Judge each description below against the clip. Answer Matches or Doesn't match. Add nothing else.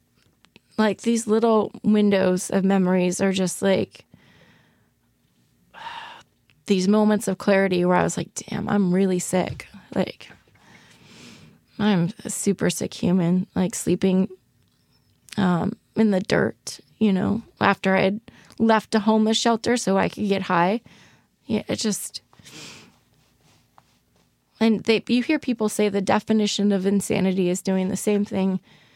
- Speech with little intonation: Matches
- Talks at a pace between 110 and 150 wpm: Matches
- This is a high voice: Matches